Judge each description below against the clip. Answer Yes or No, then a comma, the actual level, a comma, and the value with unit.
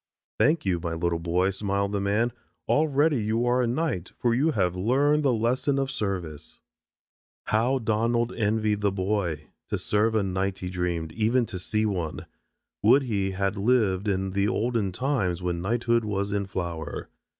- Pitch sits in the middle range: No, low, 105 Hz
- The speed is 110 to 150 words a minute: No, average, 170 wpm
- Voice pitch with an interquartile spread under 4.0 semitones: No, average, 4.3 semitones